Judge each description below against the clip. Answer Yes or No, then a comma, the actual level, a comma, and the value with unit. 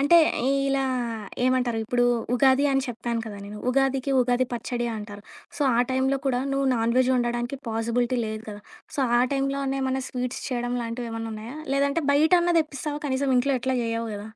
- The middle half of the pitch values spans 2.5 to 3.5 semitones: Yes, average, 2.8 semitones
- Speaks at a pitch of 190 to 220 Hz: No, very high, 250 Hz